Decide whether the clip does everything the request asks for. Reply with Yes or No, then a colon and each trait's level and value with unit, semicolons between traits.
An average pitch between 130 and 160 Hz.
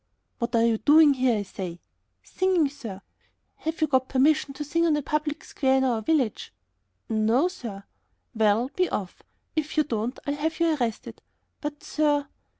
No: very high, 275 Hz